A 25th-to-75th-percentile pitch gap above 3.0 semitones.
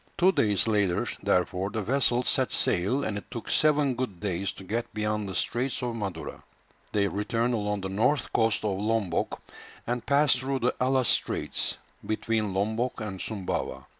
Yes: average, 3.8 semitones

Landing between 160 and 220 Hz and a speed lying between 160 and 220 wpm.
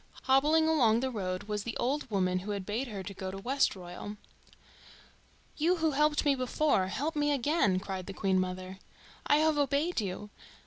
No: high, 230 Hz; average, 175 wpm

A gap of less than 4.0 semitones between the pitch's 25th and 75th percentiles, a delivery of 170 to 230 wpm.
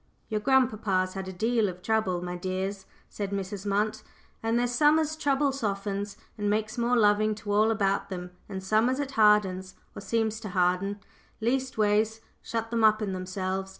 Yes: average, 2.8 semitones; average, 185 wpm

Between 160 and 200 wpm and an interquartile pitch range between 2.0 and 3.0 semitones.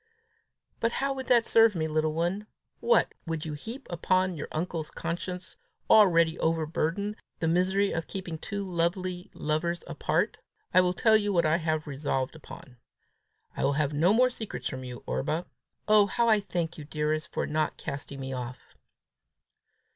No: average, 165 wpm; average, 4.4 semitones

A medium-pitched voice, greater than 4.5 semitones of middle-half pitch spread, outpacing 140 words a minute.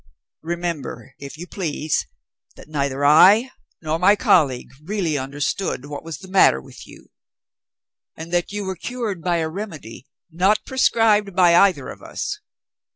Yes: medium, 170 Hz; average, 5.0 semitones; average, 150 wpm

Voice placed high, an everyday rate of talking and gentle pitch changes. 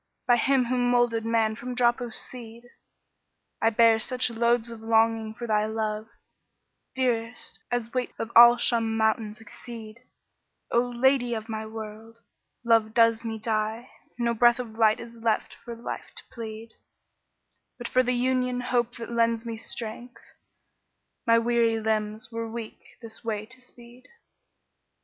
Yes: high, 230 Hz; average, 160 wpm; narrow, 1.5 semitones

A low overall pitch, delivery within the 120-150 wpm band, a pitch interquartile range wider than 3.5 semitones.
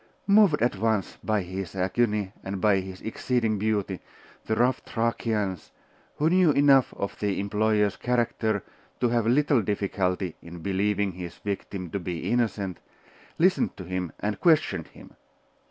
Yes: low, 105 Hz; average, 145 wpm; average, 3.9 semitones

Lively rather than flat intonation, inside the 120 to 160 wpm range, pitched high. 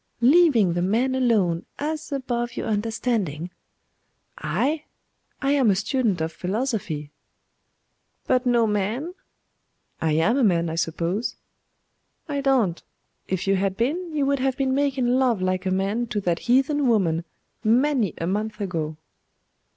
Yes: wide, 6.1 semitones; average, 145 wpm; high, 225 Hz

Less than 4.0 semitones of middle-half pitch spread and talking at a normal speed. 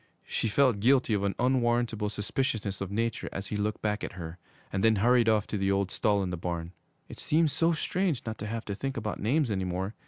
No: average, 3.6 semitones; fast, 230 wpm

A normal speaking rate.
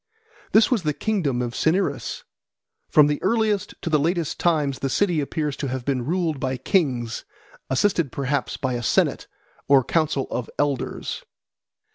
Yes: average, 155 wpm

